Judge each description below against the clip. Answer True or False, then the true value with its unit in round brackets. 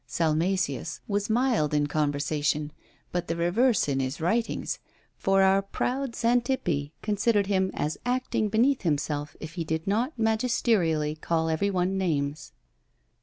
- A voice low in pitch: False (180 Hz)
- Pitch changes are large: True (6.3 semitones)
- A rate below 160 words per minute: True (135 wpm)